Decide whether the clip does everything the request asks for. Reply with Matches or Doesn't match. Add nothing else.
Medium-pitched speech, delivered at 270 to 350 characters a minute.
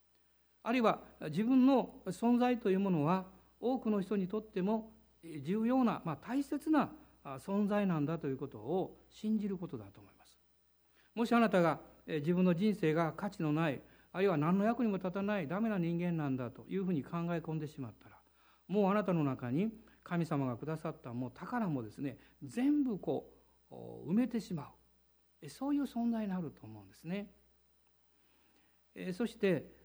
Matches